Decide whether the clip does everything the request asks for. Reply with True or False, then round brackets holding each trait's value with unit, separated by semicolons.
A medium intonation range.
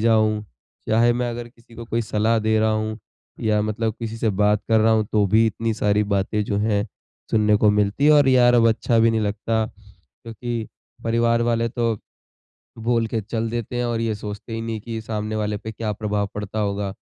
False (1.6 semitones)